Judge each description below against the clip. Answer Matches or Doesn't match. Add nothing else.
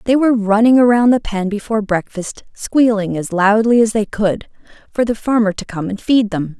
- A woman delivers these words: Matches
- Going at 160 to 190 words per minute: Doesn't match